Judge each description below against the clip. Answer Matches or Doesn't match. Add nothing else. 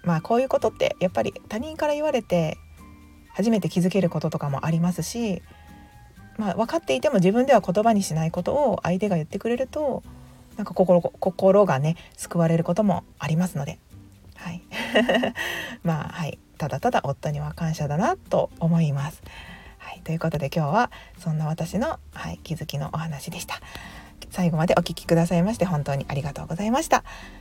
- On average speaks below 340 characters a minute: Doesn't match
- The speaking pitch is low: Doesn't match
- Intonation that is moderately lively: Matches